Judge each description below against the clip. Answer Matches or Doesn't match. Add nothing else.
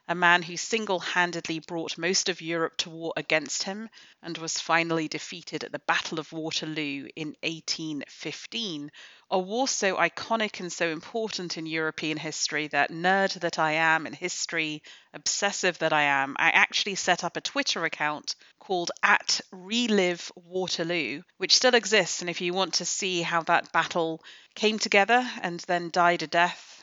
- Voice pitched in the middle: Matches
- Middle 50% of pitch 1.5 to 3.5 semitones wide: Matches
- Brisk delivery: Doesn't match